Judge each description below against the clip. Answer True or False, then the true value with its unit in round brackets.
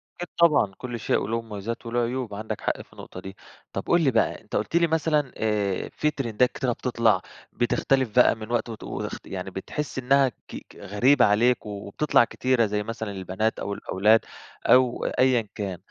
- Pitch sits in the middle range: False (115 Hz)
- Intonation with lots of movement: False (3.8 semitones)